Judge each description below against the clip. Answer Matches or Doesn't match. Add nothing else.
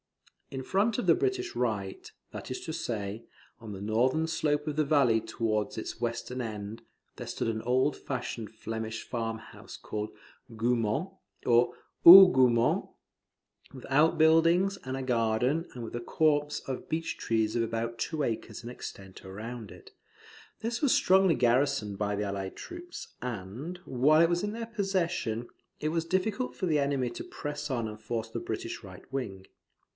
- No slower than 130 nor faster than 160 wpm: Doesn't match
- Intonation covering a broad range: Matches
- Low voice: Matches